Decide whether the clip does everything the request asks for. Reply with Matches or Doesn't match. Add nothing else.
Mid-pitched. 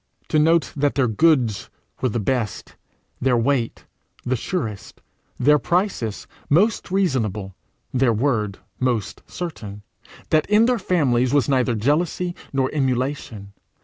Doesn't match